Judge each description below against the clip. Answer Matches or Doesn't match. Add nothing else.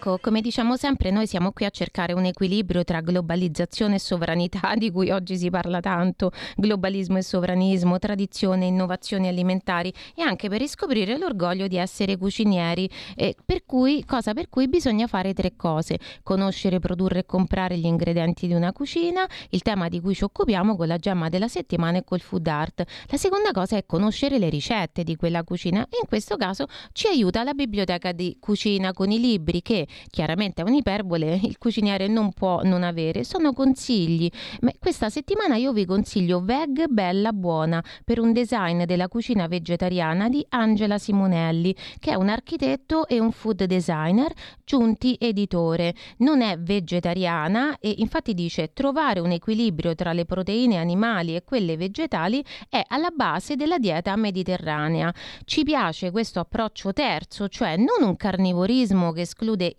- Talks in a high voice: Matches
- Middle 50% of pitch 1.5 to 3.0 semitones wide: Doesn't match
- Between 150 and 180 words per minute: Matches